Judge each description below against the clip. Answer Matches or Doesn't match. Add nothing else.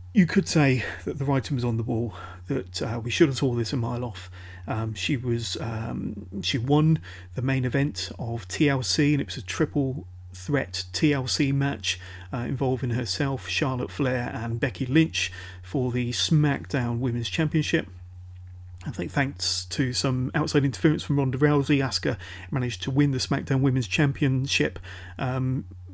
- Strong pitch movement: Matches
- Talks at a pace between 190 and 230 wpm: Doesn't match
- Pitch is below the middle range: Matches